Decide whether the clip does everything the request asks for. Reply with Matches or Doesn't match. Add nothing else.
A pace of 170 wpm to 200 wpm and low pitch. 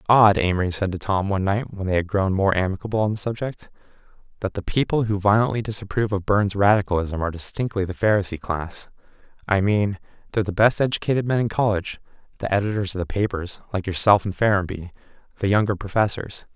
Matches